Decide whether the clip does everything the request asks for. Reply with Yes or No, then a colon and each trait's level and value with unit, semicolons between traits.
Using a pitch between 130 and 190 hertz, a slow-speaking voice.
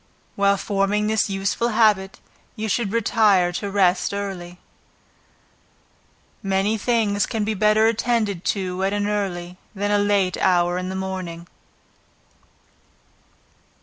No: high, 200 Hz; slow, 120 wpm